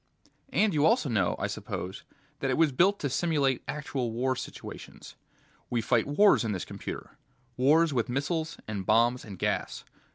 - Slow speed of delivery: No, average, 165 wpm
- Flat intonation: No, average, 5.3 semitones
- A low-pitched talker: Yes, low, 130 Hz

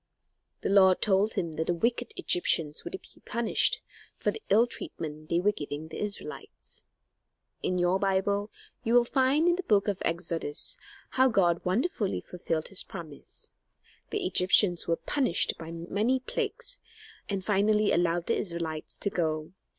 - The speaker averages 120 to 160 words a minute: Yes, average, 155 wpm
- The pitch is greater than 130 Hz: Yes, high, 190 Hz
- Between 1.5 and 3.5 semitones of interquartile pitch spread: No, average, 5.1 semitones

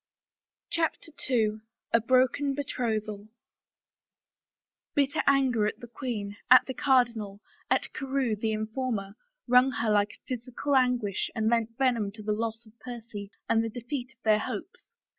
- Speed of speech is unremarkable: Yes, average, 145 wpm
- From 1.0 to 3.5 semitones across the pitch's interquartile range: Yes, average, 3.1 semitones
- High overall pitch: Yes, high, 235 Hz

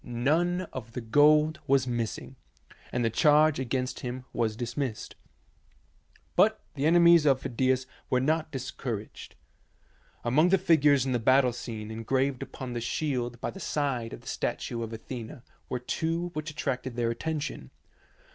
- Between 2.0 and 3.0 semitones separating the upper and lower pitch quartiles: No, average, 4.1 semitones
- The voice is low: Yes, low, 130 Hz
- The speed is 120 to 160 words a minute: Yes, average, 150 wpm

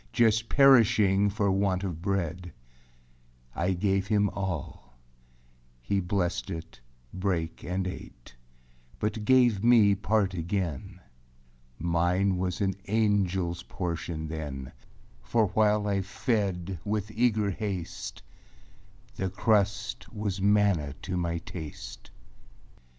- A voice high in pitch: No, very low, 95 Hz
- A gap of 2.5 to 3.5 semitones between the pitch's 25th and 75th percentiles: Yes, average, 3.2 semitones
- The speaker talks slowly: Yes, slow, 105 wpm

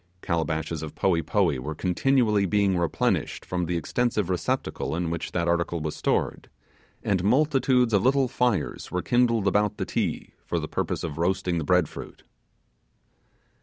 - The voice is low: Yes, very low, 90 Hz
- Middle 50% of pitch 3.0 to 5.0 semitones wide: Yes, average, 4.5 semitones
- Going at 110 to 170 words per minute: Yes, average, 160 wpm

